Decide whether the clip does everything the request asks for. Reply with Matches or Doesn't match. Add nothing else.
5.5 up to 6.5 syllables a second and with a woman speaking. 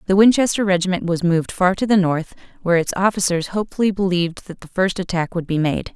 Matches